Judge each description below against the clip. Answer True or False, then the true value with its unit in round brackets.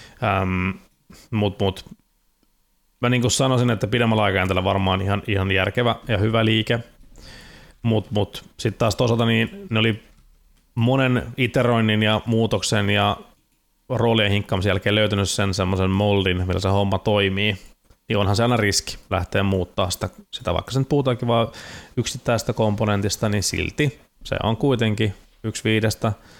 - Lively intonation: False (3.0 semitones)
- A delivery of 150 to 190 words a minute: False (140 wpm)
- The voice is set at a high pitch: False (105 Hz)